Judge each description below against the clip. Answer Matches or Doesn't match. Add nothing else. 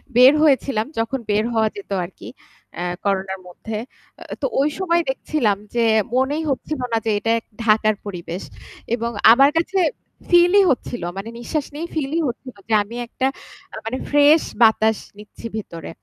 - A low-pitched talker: Doesn't match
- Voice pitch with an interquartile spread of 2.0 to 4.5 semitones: Doesn't match